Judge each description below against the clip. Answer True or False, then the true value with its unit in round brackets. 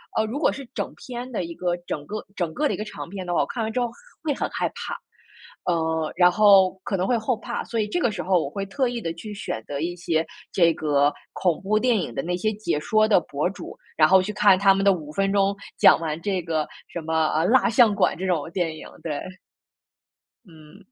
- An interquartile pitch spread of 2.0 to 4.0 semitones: False (4.7 semitones)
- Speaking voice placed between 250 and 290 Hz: False (190 Hz)